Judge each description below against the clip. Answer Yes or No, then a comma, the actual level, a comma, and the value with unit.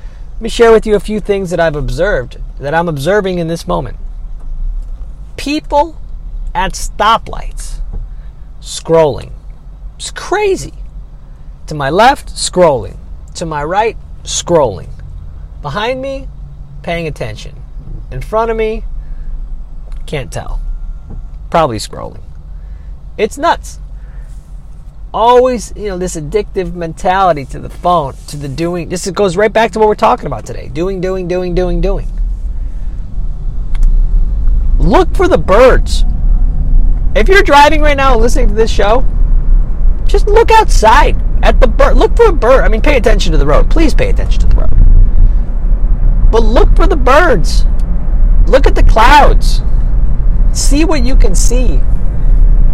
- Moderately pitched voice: Yes, medium, 170 Hz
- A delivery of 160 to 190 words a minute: No, average, 140 wpm